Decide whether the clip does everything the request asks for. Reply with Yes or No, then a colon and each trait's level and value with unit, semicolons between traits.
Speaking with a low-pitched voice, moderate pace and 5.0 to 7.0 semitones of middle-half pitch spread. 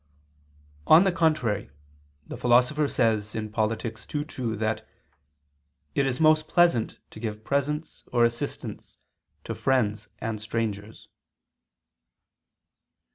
No: low, 120 Hz; slow, 105 wpm; average, 5.3 semitones